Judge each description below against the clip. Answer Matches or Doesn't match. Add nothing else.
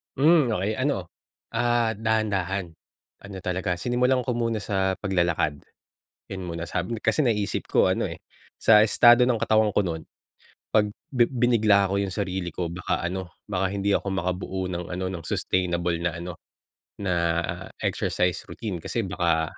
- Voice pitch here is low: Matches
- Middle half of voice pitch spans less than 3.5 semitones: Doesn't match